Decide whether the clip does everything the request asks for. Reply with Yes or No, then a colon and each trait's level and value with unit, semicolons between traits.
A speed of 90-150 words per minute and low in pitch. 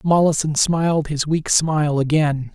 No: average, 140 wpm; medium, 150 Hz